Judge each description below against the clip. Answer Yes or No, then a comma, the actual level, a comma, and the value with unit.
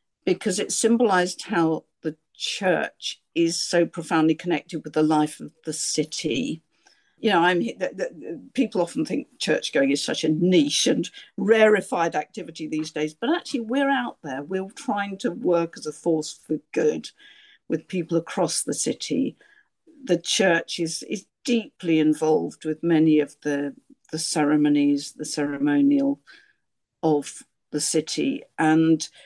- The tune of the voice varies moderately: No, wide, 6.5 semitones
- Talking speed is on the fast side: No, average, 145 wpm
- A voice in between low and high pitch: Yes, medium, 165 Hz